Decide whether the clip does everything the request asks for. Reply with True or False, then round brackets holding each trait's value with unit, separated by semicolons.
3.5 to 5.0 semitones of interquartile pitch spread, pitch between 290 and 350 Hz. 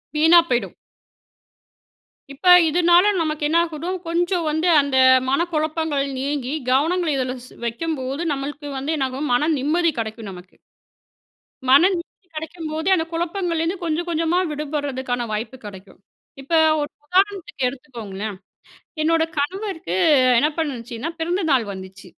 True (4.3 semitones; 300 Hz)